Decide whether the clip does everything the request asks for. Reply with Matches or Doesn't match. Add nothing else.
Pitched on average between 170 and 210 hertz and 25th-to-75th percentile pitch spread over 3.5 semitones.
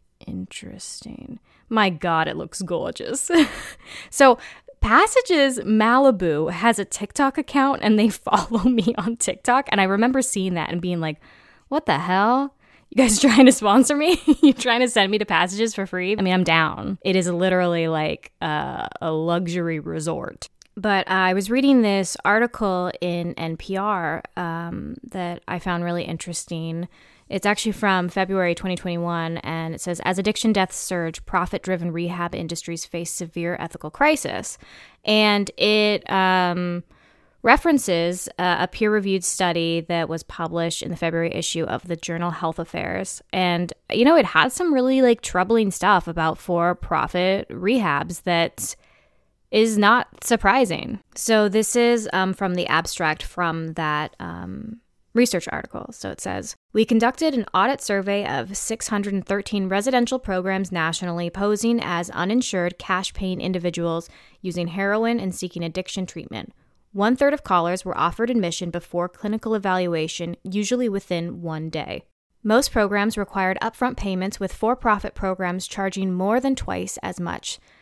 Matches